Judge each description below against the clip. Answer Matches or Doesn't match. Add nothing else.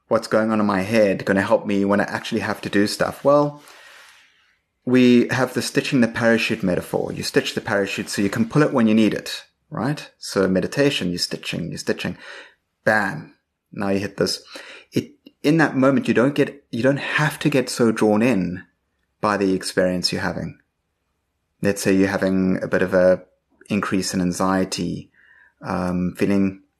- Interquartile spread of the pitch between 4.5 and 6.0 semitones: Doesn't match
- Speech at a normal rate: Matches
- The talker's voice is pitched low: Matches